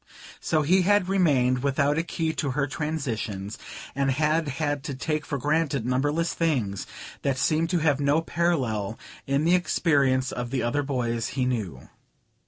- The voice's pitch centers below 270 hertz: Yes, medium, 140 Hz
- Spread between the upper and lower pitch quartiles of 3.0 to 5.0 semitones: Yes, average, 4.0 semitones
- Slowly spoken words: No, average, 165 wpm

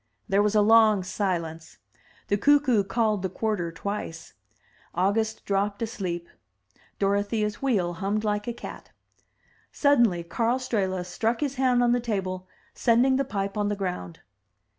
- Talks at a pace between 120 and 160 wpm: Yes, average, 140 wpm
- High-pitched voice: Yes, high, 205 Hz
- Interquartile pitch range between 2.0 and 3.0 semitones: No, average, 3.5 semitones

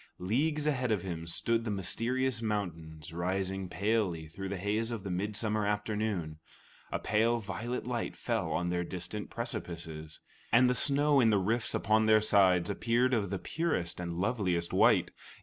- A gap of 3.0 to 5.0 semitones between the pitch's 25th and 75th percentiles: Yes, average, 4.5 semitones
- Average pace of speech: Yes, average, 165 wpm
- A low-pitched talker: Yes, low, 105 Hz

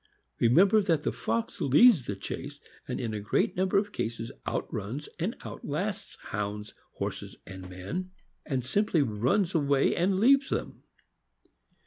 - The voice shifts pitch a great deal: Yes, wide, 9.0 semitones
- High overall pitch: No, medium, 140 Hz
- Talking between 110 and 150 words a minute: Yes, average, 140 wpm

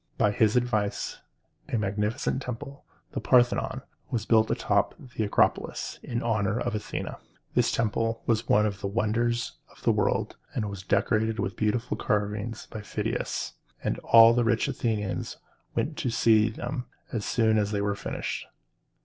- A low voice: Yes, low, 110 Hz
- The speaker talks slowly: No, average, 160 wpm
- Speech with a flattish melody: Yes, narrow, 2.3 semitones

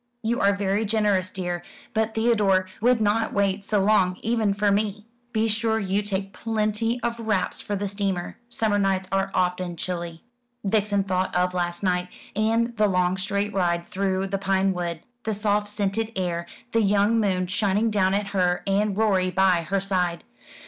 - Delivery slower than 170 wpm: No, average, 175 wpm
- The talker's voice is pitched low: No, high, 200 Hz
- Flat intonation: Yes, narrow, 2.3 semitones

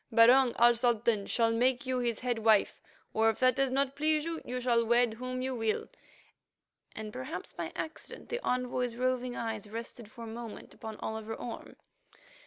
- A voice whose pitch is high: Yes, high, 240 Hz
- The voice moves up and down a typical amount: No, narrow, 2.2 semitones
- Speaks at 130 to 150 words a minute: No, average, 175 wpm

